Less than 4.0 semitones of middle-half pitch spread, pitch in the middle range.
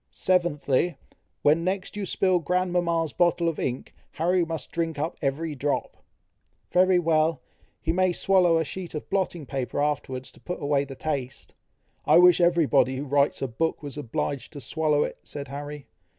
Yes: average, 3.5 semitones; medium, 160 Hz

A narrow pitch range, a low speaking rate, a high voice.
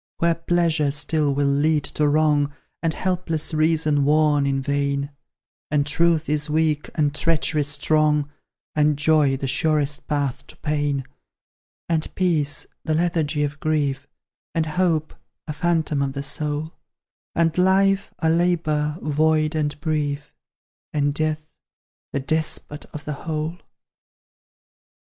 No: narrow, 1.7 semitones; slow, 130 wpm; medium, 150 Hz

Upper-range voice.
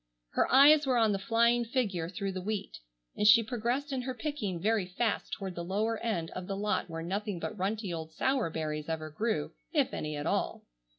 Yes: high, 205 Hz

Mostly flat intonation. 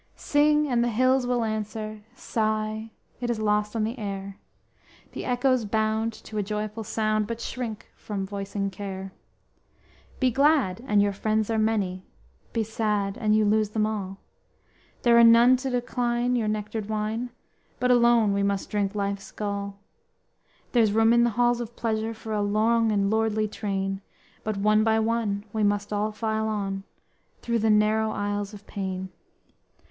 Yes: narrow, 2.1 semitones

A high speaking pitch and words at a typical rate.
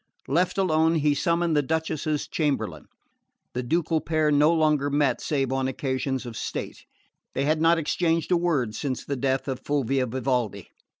No: medium, 145 Hz; average, 165 wpm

